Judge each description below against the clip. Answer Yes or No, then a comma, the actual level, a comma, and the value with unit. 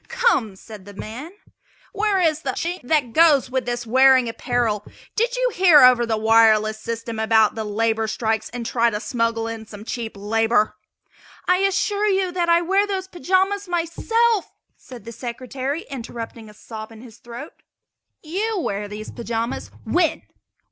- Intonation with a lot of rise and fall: Yes, wide, 7.7 semitones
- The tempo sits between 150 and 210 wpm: Yes, average, 160 wpm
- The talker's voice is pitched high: Yes, high, 245 Hz